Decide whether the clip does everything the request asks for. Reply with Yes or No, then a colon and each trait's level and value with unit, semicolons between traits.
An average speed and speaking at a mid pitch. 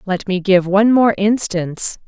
No: average, 175 wpm; high, 195 Hz